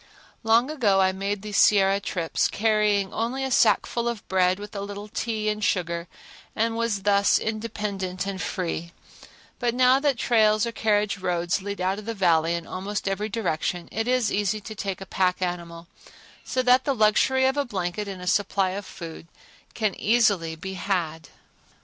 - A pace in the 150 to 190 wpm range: Yes, average, 180 wpm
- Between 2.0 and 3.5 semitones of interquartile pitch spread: Yes, average, 3.2 semitones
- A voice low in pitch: No, high, 200 Hz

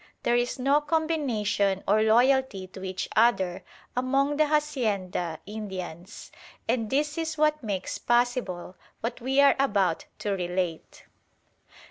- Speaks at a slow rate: Yes, slow, 125 wpm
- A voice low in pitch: No, high, 230 Hz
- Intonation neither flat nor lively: No, wide, 6.3 semitones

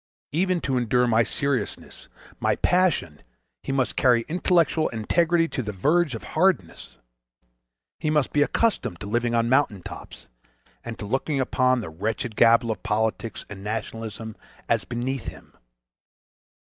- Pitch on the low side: Yes, low, 120 Hz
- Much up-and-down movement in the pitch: No, average, 4.9 semitones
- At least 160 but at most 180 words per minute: No, average, 140 wpm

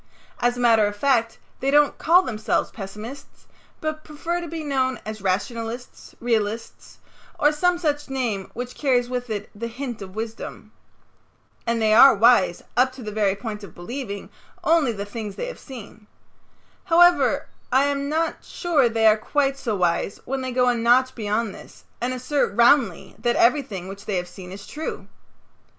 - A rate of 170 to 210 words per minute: Yes, average, 175 wpm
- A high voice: Yes, high, 240 Hz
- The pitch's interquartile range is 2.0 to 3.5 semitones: No, average, 4.6 semitones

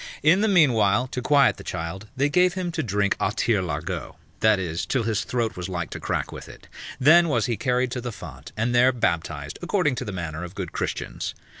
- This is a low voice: Yes, low, 115 Hz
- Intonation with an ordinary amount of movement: No, wide, 6.8 semitones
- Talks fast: Yes, fast, 215 wpm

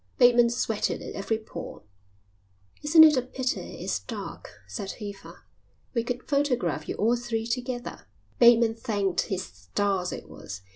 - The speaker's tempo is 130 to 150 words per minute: Yes, average, 145 wpm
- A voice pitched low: No, high, 235 Hz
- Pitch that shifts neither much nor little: Yes, average, 3.4 semitones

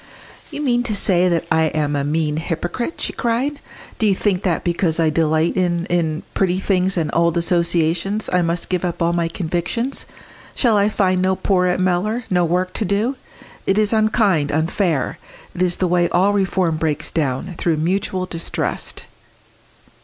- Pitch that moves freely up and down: No, average, 2.9 semitones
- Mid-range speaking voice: Yes, medium, 180 Hz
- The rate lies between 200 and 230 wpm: No, average, 175 wpm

